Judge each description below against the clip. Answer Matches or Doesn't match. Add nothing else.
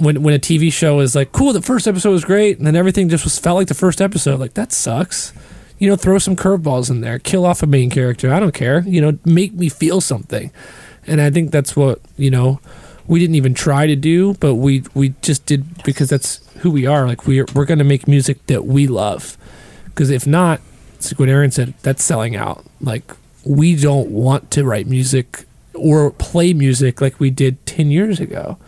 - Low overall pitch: Doesn't match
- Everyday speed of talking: Doesn't match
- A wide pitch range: Doesn't match